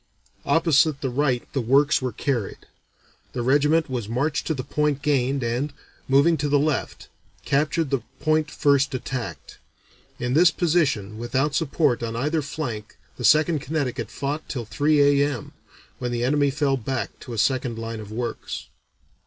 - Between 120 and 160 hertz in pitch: Yes, medium, 140 Hz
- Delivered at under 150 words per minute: No, average, 160 wpm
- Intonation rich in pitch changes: No, average, 3.4 semitones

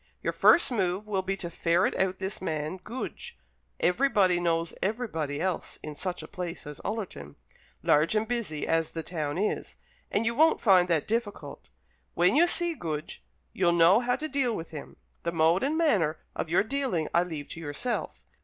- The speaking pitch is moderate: Yes, medium, 180 Hz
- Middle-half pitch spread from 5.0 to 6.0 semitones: Yes, wide, 5.4 semitones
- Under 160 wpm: No, average, 180 wpm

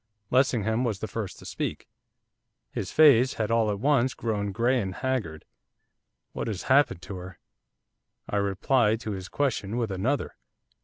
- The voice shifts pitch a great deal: No, average, 4.3 semitones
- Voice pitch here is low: Yes, low, 110 Hz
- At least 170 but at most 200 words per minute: No, average, 155 wpm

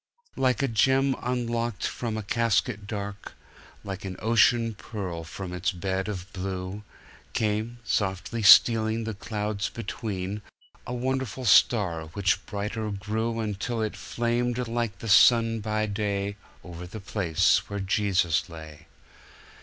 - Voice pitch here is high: No, low, 105 Hz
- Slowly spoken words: Yes, slow, 130 wpm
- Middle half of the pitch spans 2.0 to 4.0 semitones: Yes, average, 3.1 semitones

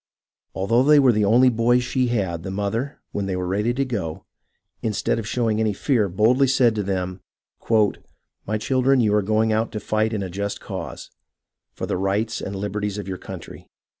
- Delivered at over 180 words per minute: Yes, average, 195 wpm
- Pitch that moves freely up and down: No, average, 3.3 semitones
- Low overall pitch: Yes, low, 110 Hz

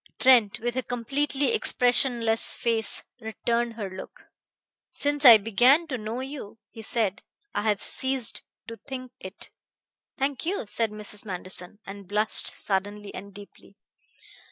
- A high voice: Yes, high, 230 Hz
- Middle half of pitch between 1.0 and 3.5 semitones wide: No, average, 3.9 semitones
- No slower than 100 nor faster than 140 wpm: Yes, slow, 135 wpm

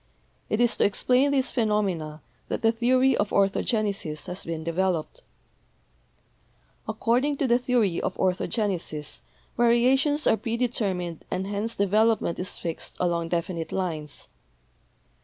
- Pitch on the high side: Yes, high, 205 Hz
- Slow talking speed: Yes, slow, 125 wpm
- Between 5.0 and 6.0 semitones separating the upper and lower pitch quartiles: Yes, average, 5.3 semitones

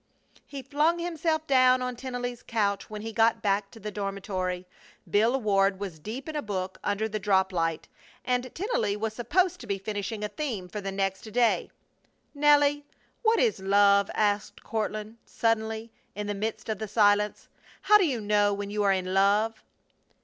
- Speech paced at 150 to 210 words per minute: Yes, average, 180 wpm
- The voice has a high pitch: Yes, high, 215 Hz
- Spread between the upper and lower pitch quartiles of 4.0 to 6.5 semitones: No, average, 3.6 semitones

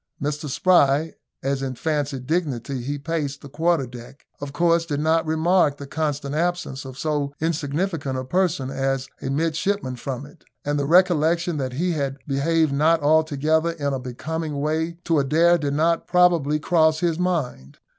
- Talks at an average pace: Yes, average, 165 wpm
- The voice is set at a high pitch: No, medium, 150 Hz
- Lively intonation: No, average, 3.2 semitones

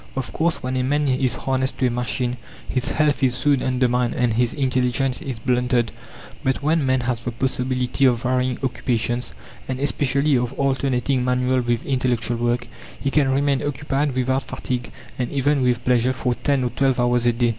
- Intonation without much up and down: Yes, narrow, 1.6 semitones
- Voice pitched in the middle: No, low, 130 Hz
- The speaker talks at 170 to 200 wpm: Yes, average, 185 wpm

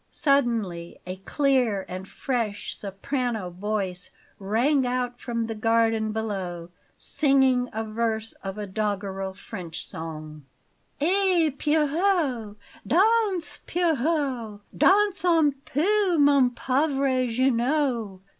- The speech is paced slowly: Yes, slow, 100 wpm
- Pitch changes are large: Yes, wide, 6.0 semitones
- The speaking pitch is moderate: No, high, 240 Hz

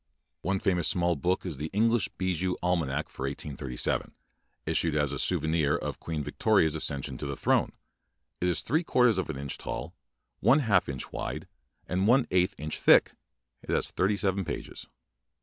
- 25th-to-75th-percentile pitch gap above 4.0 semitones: Yes, average, 4.5 semitones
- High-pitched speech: No, very low, 85 Hz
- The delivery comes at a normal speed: Yes, average, 180 wpm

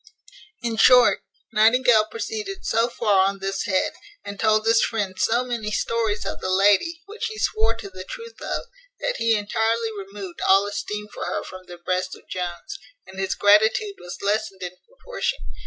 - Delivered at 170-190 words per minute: Yes, average, 175 wpm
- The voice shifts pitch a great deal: No, average, 3.2 semitones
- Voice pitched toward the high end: Yes, high, 215 Hz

